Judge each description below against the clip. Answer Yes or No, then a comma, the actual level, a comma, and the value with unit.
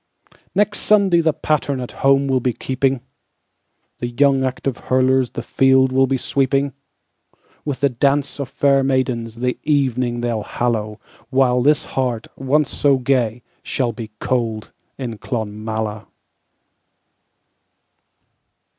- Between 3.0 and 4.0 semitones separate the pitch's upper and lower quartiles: No, narrow, 2.5 semitones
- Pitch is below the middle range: Yes, low, 130 Hz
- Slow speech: Yes, slow, 105 wpm